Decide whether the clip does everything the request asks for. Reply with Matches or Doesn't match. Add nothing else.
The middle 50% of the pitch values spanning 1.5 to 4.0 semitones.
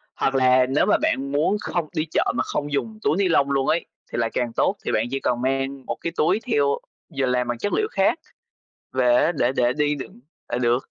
Matches